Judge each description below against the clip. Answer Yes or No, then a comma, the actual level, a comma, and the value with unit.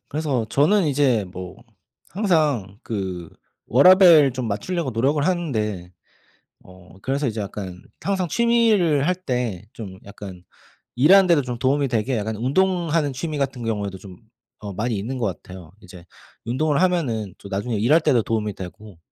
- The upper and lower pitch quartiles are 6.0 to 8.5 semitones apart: Yes, wide, 7.3 semitones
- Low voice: Yes, low, 125 Hz